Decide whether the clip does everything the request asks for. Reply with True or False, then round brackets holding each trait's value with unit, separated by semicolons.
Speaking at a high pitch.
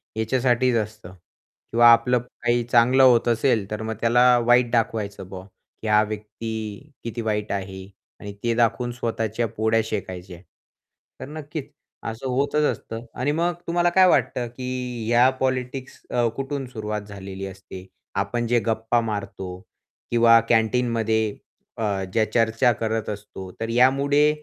False (115 Hz)